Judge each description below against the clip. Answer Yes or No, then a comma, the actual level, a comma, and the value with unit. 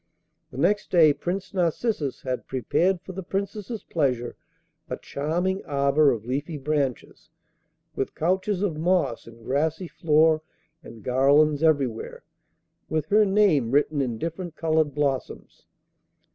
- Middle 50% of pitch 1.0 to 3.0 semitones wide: No, average, 4.8 semitones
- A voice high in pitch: No, medium, 155 Hz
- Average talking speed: No, slow, 130 wpm